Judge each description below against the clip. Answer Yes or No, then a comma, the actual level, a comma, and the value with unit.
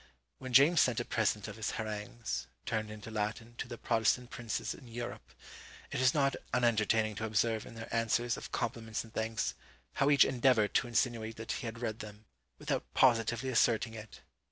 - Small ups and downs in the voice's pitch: Yes, narrow, 1.7 semitones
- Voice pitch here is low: Yes, low, 115 Hz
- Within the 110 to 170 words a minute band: No, average, 180 wpm